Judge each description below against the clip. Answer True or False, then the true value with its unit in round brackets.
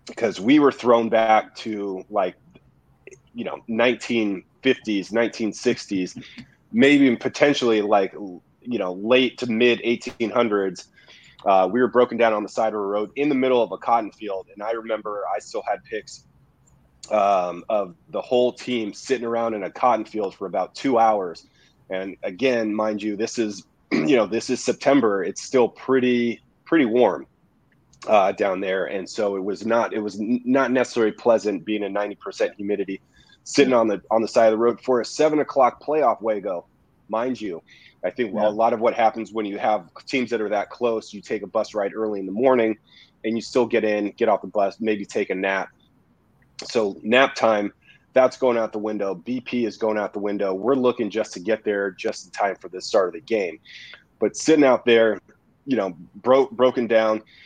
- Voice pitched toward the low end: True (115 Hz)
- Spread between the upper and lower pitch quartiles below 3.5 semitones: True (3.0 semitones)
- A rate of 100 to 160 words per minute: False (200 wpm)